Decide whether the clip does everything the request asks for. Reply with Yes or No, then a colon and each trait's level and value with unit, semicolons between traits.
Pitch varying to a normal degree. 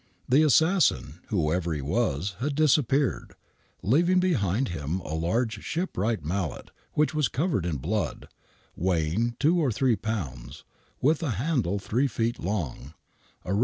No: wide, 8.6 semitones